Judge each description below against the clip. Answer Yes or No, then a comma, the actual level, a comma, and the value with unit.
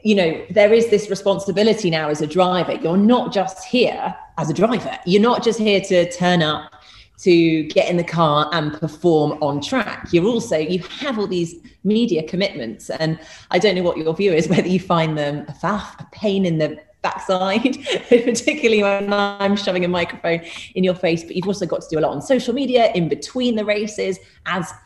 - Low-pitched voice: No, medium, 185 Hz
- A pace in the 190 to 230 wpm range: Yes, fast, 205 wpm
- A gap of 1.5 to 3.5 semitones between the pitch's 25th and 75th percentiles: No, average, 4.1 semitones